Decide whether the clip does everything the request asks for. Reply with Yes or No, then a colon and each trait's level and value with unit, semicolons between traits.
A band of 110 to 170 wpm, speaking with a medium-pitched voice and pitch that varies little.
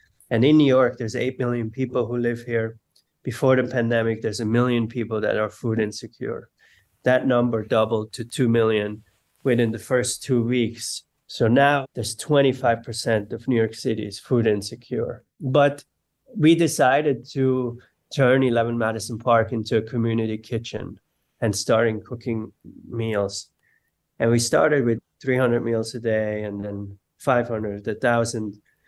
No: average, 150 wpm; low, 115 Hz; narrow, 2.3 semitones